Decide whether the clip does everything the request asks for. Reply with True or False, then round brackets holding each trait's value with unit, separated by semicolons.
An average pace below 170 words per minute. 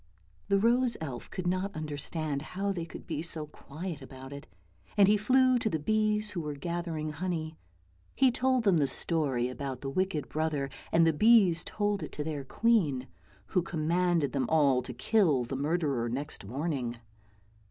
False (175 wpm)